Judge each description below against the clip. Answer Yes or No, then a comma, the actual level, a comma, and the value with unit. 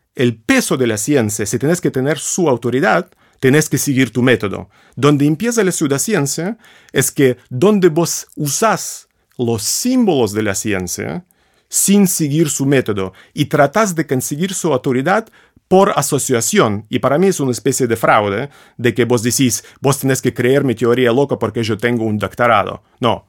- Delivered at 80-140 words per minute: No, average, 175 wpm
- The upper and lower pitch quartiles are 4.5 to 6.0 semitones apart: Yes, average, 4.9 semitones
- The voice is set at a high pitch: No, low, 135 Hz